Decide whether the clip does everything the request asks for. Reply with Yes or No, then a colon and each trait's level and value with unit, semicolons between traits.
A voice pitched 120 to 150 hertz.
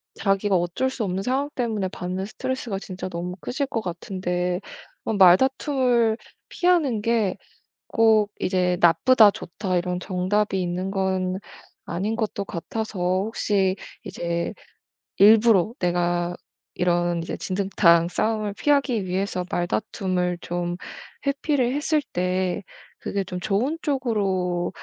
No: high, 195 Hz